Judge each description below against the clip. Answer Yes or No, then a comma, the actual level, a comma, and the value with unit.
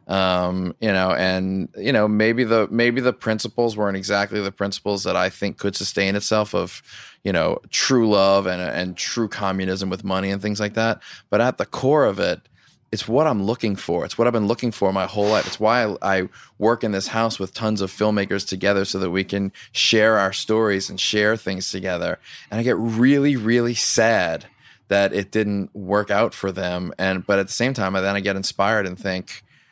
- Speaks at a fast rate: Yes, fast, 215 wpm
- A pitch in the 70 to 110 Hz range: Yes, low, 100 Hz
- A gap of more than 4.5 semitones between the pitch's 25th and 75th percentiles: No, narrow, 2.5 semitones